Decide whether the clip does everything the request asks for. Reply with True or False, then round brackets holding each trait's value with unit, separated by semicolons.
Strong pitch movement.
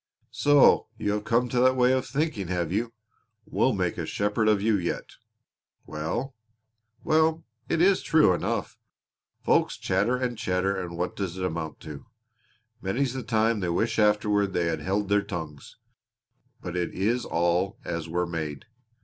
True (5.8 semitones)